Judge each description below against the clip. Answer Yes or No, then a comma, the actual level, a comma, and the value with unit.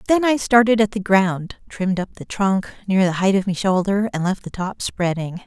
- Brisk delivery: Yes, fast, 230 wpm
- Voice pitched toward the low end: No, high, 195 Hz